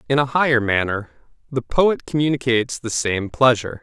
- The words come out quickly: No, average, 155 wpm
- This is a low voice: Yes, low, 125 Hz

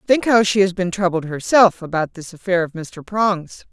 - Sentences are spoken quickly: Yes, fast, 210 wpm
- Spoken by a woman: Yes, female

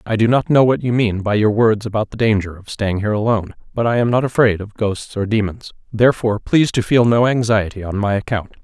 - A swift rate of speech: Yes, fast, 245 wpm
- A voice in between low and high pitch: No, low, 110 Hz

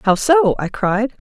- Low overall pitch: No, high, 235 Hz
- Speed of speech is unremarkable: Yes, average, 190 wpm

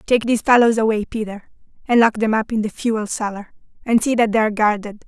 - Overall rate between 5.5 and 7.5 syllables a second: Yes, 6.1 syllables/s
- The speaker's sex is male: No, female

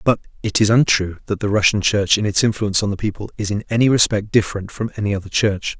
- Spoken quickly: Yes, fast, 240 wpm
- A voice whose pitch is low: Yes, low, 105 Hz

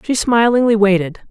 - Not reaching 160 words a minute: Yes, average, 140 wpm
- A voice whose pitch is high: Yes, high, 215 Hz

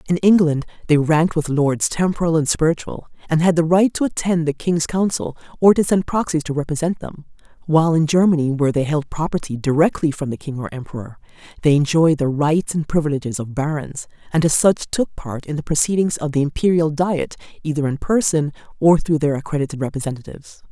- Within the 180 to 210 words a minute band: Yes, average, 190 wpm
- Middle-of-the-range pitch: Yes, medium, 155 Hz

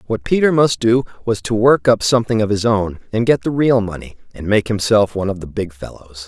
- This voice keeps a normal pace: No, fast, 240 wpm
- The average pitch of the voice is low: Yes, low, 110 Hz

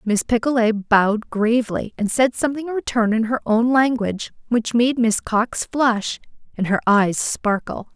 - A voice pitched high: Yes, high, 230 Hz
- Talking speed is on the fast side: No, average, 165 wpm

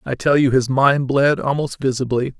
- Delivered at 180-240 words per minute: Yes, average, 200 wpm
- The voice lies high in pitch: No, low, 135 Hz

